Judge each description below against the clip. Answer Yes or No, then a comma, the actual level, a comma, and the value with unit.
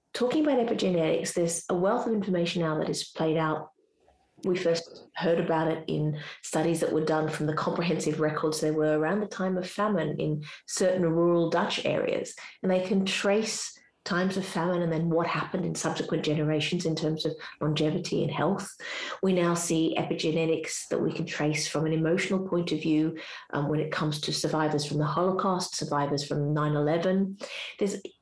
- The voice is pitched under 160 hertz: No, medium, 165 Hz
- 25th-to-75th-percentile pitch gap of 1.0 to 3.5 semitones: Yes, average, 3.1 semitones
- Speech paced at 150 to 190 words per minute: Yes, average, 185 wpm